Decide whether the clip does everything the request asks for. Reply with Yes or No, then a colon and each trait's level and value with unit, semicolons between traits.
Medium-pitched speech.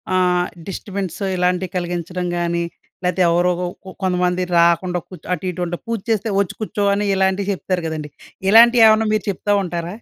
Yes: medium, 180 Hz